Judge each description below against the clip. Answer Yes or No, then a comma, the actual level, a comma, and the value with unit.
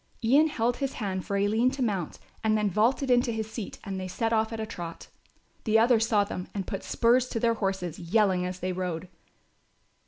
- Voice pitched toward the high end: Yes, high, 215 Hz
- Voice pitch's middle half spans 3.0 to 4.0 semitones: Yes, average, 3.7 semitones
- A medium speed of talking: No, fast, 210 wpm